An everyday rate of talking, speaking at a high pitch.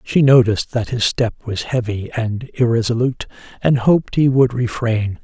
No: average, 160 wpm; low, 120 Hz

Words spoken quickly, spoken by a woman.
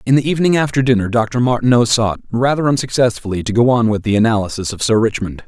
No: fast, 210 wpm; male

